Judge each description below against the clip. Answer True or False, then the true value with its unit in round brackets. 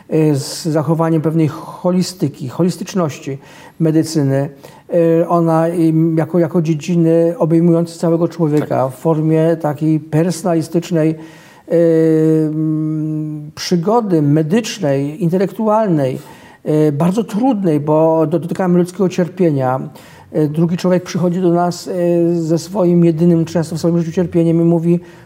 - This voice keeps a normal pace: False (95 wpm)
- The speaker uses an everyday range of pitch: False (1.8 semitones)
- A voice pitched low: False (165 Hz)